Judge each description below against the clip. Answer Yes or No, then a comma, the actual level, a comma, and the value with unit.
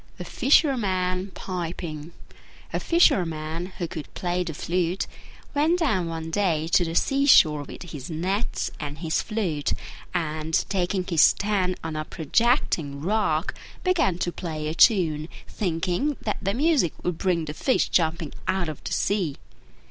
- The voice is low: No, medium, 175 Hz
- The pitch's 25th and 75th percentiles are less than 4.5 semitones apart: Yes, average, 3.9 semitones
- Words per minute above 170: No, average, 150 wpm